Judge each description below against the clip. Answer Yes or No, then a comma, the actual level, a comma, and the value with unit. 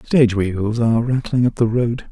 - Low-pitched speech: Yes, low, 115 Hz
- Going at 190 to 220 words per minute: Yes, average, 200 wpm